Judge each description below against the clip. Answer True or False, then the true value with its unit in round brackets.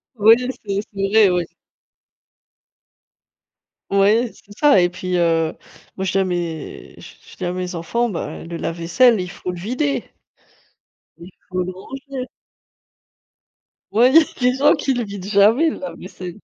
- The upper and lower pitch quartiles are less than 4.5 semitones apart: False (5.0 semitones)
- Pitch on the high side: True (195 Hz)